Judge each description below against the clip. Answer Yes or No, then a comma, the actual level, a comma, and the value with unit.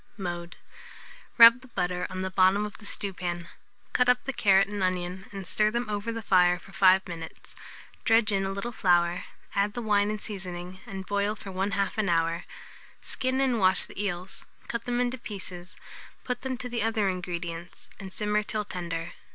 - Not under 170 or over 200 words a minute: Yes, average, 185 wpm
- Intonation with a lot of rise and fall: No, average, 3.2 semitones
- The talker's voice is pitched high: Yes, high, 195 Hz